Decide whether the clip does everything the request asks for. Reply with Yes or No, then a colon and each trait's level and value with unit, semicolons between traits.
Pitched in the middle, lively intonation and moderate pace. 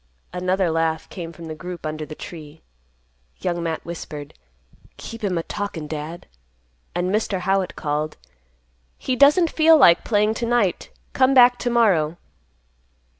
Yes: medium, 180 Hz; wide, 5.7 semitones; average, 145 wpm